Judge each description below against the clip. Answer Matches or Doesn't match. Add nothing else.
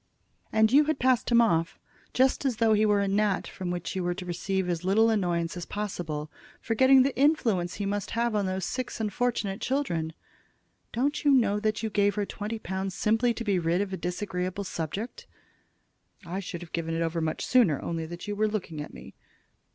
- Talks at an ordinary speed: Doesn't match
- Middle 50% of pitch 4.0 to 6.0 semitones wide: Matches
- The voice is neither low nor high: Doesn't match